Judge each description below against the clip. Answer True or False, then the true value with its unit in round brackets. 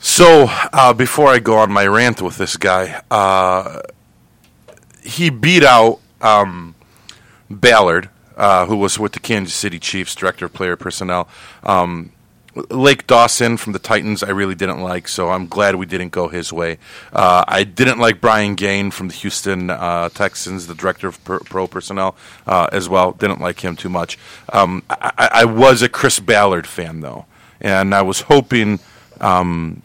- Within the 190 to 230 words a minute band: False (170 wpm)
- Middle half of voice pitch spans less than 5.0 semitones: True (3.6 semitones)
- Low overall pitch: True (95 Hz)